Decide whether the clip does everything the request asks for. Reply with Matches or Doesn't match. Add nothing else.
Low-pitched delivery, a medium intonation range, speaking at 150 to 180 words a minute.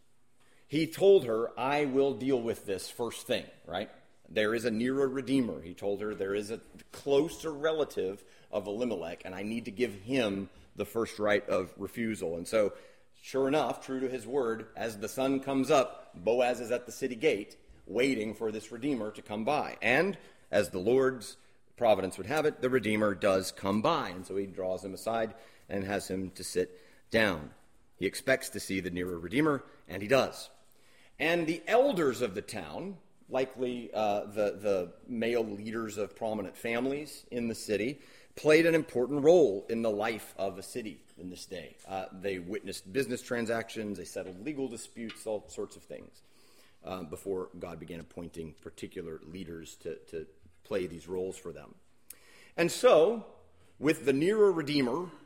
Doesn't match